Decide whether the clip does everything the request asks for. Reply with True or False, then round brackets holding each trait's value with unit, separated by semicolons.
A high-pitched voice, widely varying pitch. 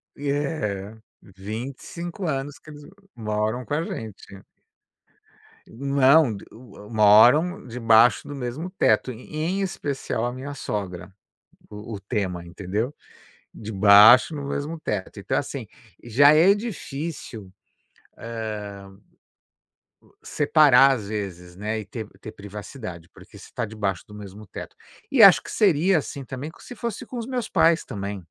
False (120 Hz; 6.3 semitones)